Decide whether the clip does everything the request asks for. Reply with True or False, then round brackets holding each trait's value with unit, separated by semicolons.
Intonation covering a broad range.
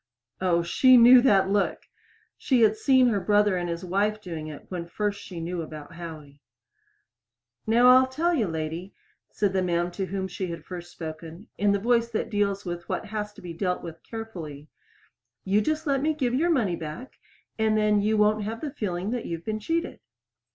False (4.7 semitones)